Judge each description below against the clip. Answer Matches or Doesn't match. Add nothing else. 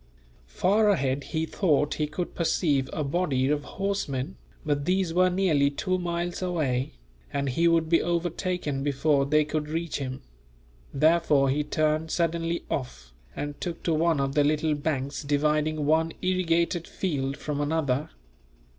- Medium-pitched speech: Matches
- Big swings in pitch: Doesn't match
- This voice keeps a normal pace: Matches